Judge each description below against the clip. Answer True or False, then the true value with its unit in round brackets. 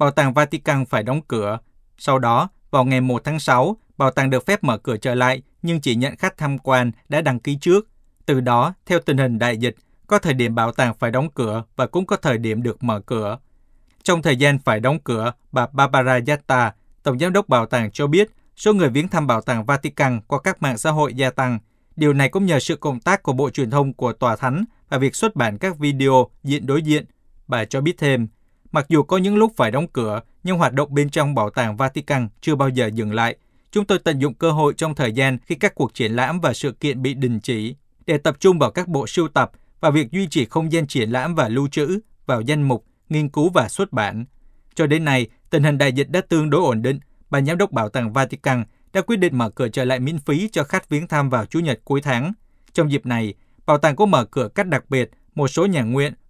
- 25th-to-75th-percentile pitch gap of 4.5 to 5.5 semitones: False (4.0 semitones)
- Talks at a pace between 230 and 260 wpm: True (245 wpm)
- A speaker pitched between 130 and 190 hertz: True (140 Hz)